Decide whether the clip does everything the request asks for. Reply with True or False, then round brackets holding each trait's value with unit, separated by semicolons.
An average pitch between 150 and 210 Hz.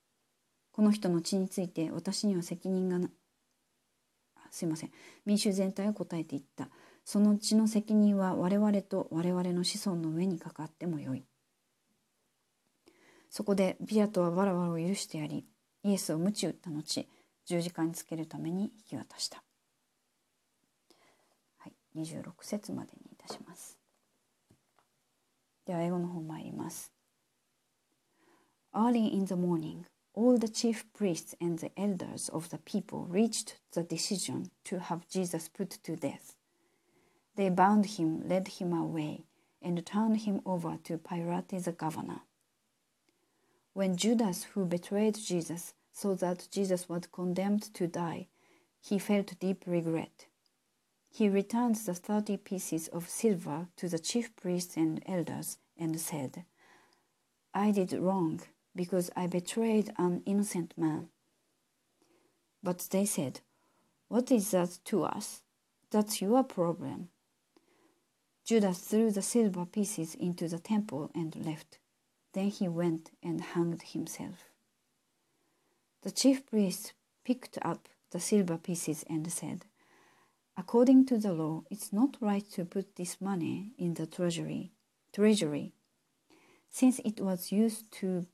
True (185 Hz)